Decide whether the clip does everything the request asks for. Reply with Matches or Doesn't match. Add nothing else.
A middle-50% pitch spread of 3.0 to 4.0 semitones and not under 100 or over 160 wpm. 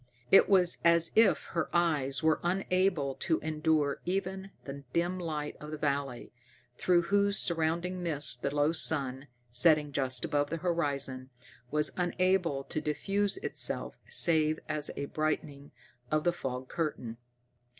Matches